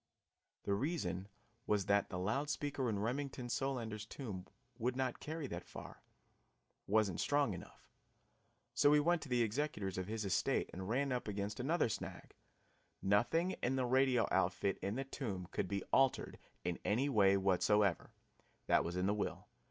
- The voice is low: Yes, low, 110 Hz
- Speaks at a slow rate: No, average, 170 wpm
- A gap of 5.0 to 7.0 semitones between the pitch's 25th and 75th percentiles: Yes, wide, 5.5 semitones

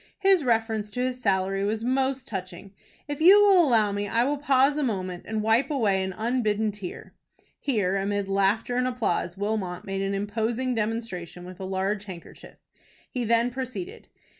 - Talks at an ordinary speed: Yes, average, 170 wpm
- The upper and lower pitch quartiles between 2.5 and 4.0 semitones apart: No, average, 4.5 semitones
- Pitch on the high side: Yes, high, 220 Hz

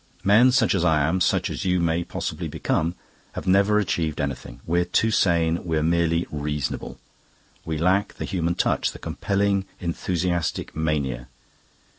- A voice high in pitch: No, very low, 85 Hz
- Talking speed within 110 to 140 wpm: No, average, 150 wpm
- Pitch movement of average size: Yes, average, 3.0 semitones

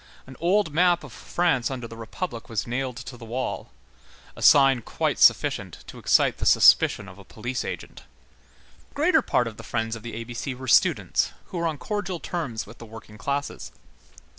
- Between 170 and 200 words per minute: Yes, average, 190 wpm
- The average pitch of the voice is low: Yes, low, 125 Hz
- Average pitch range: No, wide, 6.3 semitones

